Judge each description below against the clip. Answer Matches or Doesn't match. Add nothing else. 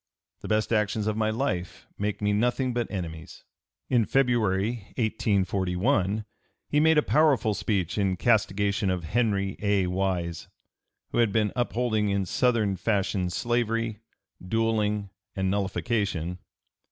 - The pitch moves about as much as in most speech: Matches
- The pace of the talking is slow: Matches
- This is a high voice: Doesn't match